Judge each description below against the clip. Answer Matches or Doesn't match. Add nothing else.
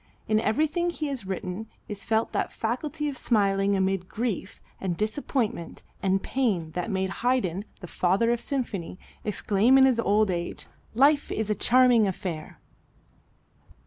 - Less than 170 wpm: Matches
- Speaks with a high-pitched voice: Matches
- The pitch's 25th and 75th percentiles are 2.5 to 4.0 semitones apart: Doesn't match